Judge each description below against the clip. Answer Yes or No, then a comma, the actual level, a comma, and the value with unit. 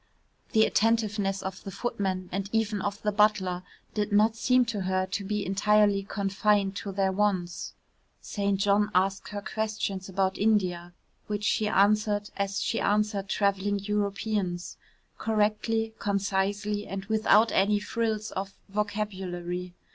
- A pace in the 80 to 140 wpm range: Yes, slow, 135 wpm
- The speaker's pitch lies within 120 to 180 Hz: No, high, 205 Hz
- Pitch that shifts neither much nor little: No, narrow, 1.6 semitones